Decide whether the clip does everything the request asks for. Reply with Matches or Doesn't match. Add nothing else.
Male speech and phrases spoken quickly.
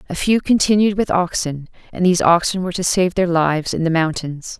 Doesn't match